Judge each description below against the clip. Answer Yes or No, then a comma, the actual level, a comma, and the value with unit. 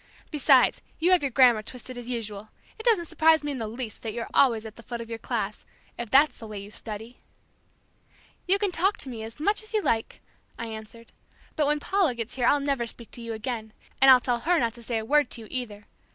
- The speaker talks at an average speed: No, fast, 235 wpm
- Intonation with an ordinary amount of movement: Yes, average, 4.5 semitones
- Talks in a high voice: Yes, high, 240 Hz